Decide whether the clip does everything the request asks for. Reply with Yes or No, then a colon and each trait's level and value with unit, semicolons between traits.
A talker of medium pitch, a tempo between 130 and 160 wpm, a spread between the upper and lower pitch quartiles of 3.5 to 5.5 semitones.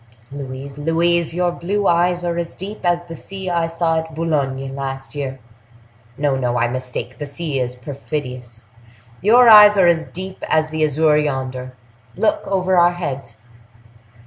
Yes: medium, 155 Hz; average, 145 wpm; average, 4.6 semitones